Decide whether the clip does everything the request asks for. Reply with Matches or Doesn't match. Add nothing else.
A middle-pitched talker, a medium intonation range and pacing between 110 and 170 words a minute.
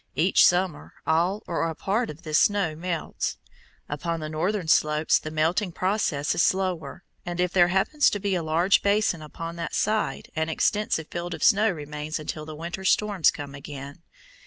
Doesn't match